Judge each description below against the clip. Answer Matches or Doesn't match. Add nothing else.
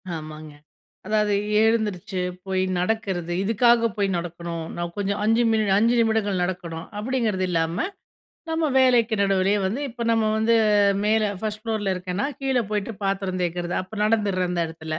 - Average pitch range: Matches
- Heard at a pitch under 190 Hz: Doesn't match